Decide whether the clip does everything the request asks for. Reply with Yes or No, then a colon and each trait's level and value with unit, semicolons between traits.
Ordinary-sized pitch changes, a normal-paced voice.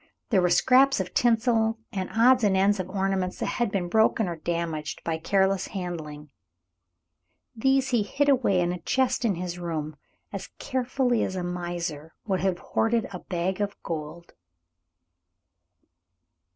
Yes: average, 4.6 semitones; average, 150 wpm